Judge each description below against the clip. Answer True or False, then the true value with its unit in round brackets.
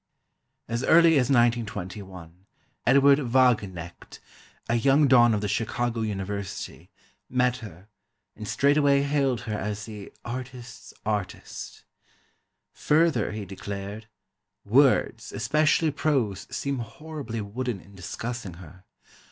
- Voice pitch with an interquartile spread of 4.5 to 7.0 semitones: True (4.8 semitones)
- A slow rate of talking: True (110 wpm)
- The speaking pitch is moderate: False (115 Hz)